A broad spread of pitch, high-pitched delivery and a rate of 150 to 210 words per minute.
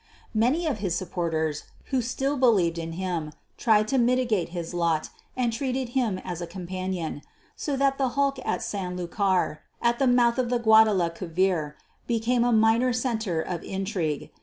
Yes: wide, 6.0 semitones; high, 210 Hz; average, 160 wpm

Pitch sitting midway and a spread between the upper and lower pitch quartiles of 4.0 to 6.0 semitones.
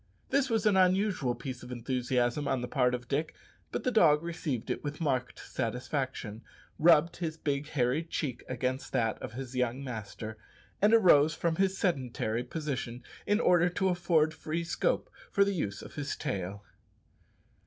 Yes: medium, 145 Hz; wide, 5.5 semitones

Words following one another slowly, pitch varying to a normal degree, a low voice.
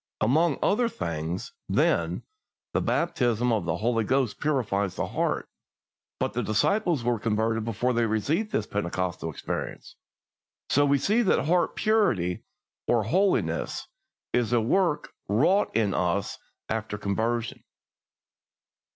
No: slow, 125 wpm; wide, 6.1 semitones; low, 115 Hz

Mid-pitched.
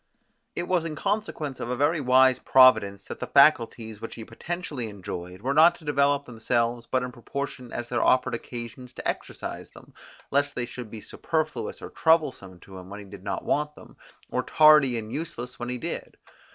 No: low, 125 Hz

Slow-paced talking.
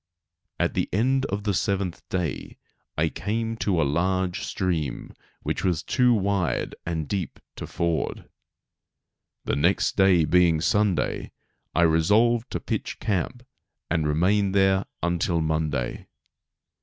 Yes: slow, 130 wpm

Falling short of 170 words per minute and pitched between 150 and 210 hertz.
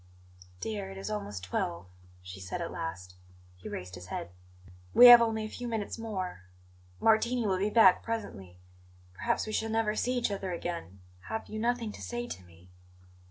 No: average, 180 wpm; high, 190 Hz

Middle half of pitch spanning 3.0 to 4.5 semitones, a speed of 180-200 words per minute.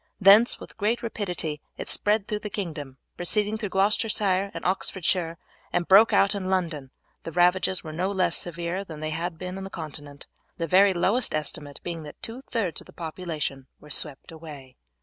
Yes: average, 4.1 semitones; average, 190 wpm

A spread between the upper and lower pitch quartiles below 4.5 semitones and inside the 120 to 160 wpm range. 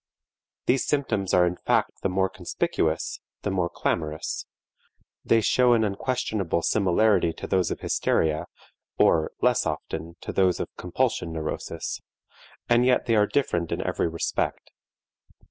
No: average, 4.9 semitones; average, 140 wpm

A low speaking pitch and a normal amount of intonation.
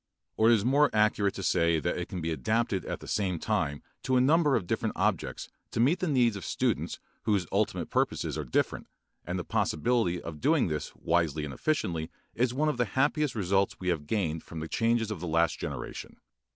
No: low, 100 Hz; wide, 6.7 semitones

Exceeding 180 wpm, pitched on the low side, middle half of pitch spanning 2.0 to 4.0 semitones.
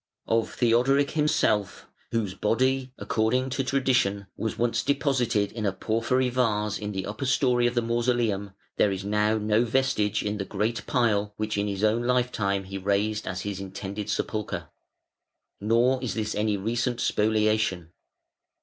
No: average, 160 wpm; low, 110 Hz; average, 3.1 semitones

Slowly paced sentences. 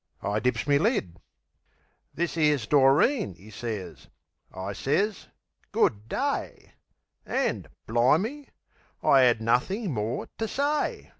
Yes: slow, 115 wpm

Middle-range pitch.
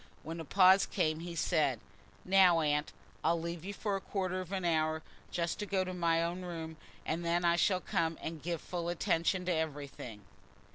Yes: medium, 170 Hz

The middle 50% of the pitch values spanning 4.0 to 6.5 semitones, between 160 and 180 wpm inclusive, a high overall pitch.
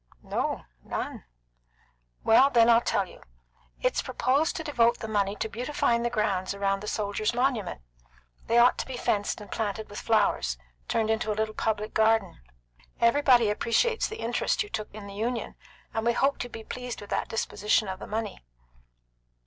No: narrow, 2.5 semitones; average, 175 wpm; high, 220 Hz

